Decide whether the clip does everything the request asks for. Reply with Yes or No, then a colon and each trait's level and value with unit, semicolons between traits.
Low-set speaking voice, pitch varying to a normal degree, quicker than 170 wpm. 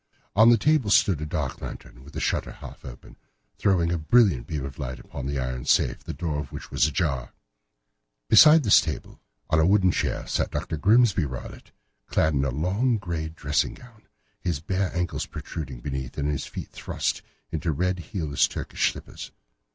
No: very low, 80 Hz; wide, 5.8 semitones; average, 180 wpm